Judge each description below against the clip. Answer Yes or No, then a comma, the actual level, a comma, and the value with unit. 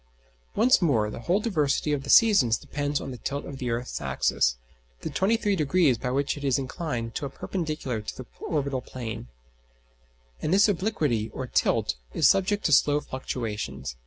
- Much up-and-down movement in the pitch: Yes, wide, 6.0 semitones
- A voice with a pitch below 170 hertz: Yes, medium, 140 Hz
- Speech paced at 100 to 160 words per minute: No, average, 170 wpm